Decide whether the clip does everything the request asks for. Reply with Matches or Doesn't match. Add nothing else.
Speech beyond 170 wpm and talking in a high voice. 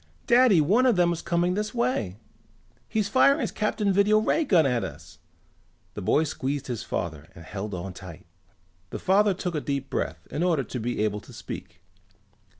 Doesn't match